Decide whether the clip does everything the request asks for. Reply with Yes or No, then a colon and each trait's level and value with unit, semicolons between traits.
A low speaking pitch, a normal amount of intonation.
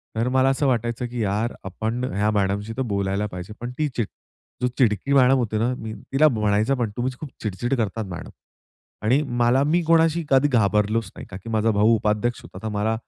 Yes: low, 115 Hz; average, 3.5 semitones